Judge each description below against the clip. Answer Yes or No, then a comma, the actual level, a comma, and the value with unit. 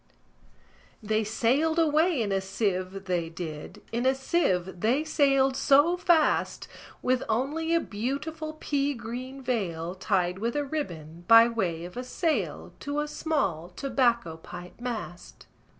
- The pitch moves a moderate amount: No, wide, 7.6 semitones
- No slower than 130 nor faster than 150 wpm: Yes, average, 145 wpm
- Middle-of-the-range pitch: No, high, 235 Hz